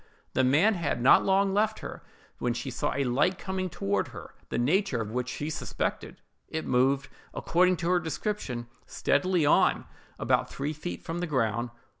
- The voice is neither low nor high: Yes, medium, 150 Hz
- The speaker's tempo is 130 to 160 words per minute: No, average, 175 wpm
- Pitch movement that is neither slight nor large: No, wide, 6.5 semitones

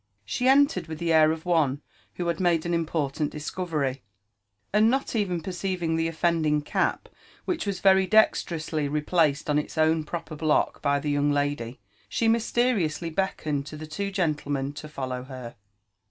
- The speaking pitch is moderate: Yes, medium, 160 Hz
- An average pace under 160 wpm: No, average, 165 wpm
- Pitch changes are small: No, average, 3.6 semitones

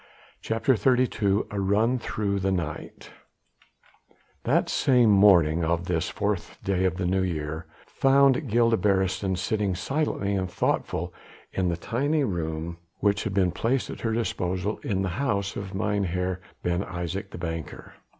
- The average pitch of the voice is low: Yes, very low, 95 Hz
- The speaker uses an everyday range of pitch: Yes, average, 3.7 semitones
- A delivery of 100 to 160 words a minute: Yes, average, 150 wpm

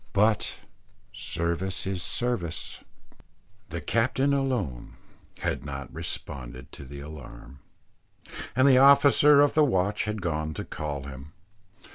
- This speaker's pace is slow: Yes, slow, 120 wpm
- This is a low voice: Yes, very low, 90 Hz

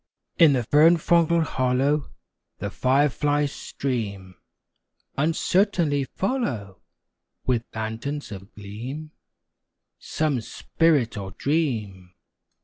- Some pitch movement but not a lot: No, wide, 5.8 semitones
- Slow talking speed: Yes, slow, 85 wpm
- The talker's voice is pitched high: No, medium, 140 Hz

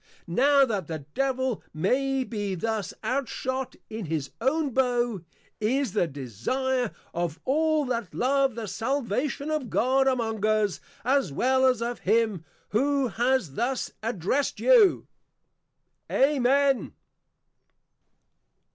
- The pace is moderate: No, slow, 115 wpm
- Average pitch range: Yes, average, 4.0 semitones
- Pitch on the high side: Yes, very high, 250 Hz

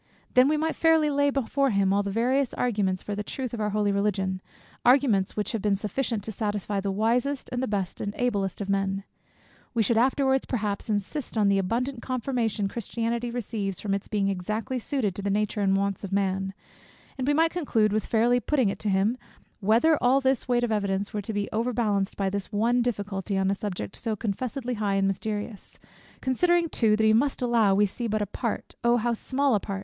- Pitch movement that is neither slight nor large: Yes, average, 3.7 semitones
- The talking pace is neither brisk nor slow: No, fast, 215 wpm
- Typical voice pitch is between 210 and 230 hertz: Yes, high, 215 Hz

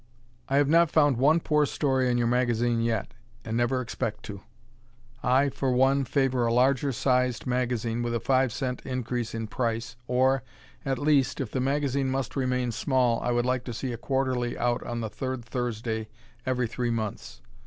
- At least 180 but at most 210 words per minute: Yes, average, 185 wpm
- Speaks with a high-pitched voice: No, low, 125 Hz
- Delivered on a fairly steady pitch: Yes, narrow, 2.0 semitones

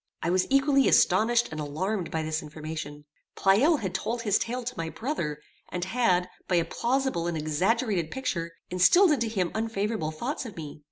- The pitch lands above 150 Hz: Yes, high, 190 Hz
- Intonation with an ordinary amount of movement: No, wide, 6.6 semitones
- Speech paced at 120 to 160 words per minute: No, average, 175 wpm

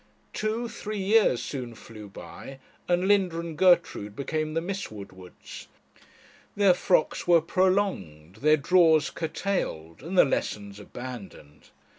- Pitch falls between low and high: Yes, medium, 160 Hz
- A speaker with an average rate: No, slow, 125 wpm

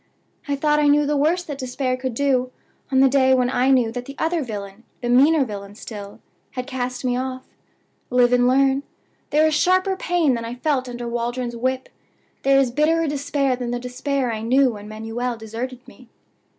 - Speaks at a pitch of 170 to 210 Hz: No, very high, 255 Hz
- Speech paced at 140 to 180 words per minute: No, average, 195 wpm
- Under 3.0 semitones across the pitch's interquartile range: Yes, narrow, 2.6 semitones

